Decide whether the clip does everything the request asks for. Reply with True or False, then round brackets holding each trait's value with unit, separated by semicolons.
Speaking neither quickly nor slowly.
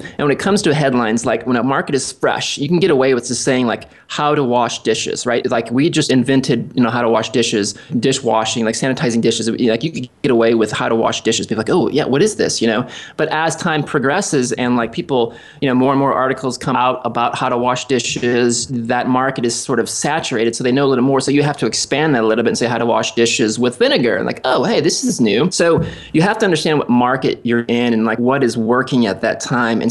False (265 wpm)